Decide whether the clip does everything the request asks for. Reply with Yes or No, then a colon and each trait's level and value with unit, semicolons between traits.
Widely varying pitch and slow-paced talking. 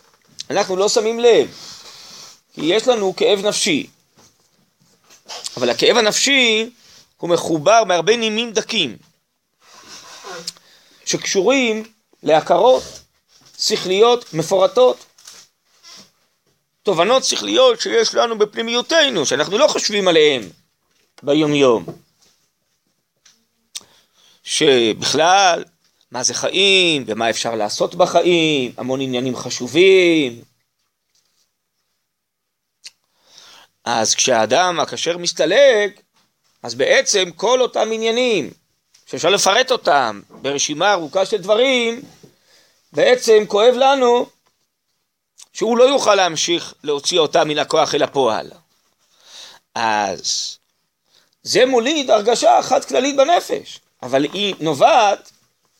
Yes: wide, 7.3 semitones; slow, 85 wpm